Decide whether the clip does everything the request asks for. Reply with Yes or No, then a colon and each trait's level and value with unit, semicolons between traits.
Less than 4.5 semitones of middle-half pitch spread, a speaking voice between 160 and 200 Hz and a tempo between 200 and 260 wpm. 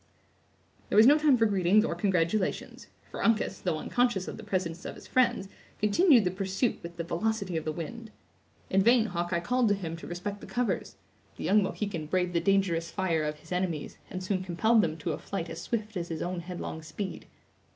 Yes: average, 4.0 semitones; high, 190 Hz; fast, 205 wpm